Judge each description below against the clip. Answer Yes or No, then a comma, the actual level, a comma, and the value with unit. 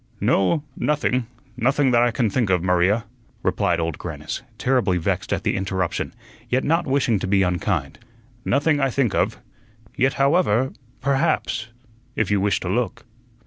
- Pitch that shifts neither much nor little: No, wide, 6.2 semitones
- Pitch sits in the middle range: No, low, 115 Hz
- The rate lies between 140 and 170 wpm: Yes, average, 155 wpm